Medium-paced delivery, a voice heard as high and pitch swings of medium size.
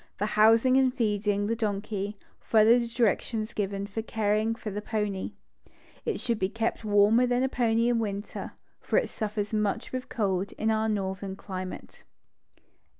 No: average, 160 wpm; high, 215 Hz; narrow, 2.0 semitones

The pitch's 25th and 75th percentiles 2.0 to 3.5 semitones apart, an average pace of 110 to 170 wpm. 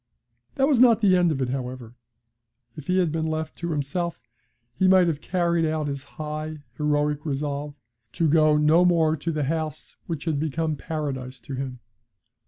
No: average, 2.7 semitones; average, 180 wpm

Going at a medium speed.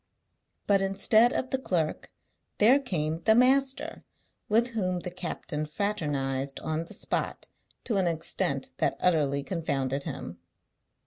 No: slow, 130 wpm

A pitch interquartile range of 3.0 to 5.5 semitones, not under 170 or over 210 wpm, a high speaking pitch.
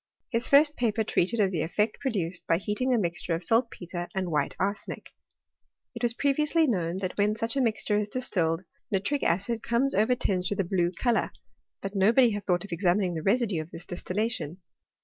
Yes: average, 4.9 semitones; average, 190 wpm; high, 205 Hz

